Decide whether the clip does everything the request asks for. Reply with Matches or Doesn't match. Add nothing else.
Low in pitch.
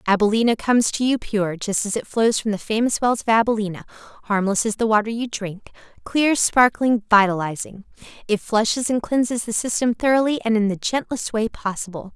Doesn't match